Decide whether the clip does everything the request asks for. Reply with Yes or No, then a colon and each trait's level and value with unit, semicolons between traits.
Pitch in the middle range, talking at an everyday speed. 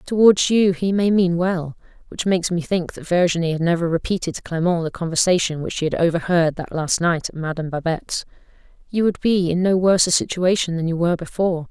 No: medium, 175 Hz; fast, 210 wpm